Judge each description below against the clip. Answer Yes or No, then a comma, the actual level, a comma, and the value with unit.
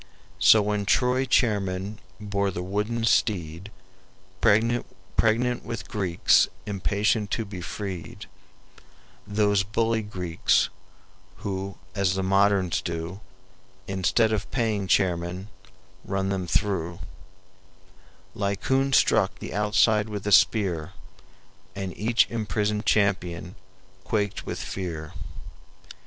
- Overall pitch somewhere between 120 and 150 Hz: No, low, 100 Hz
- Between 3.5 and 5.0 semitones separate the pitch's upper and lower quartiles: No, narrow, 2.5 semitones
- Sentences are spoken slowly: Yes, slow, 100 wpm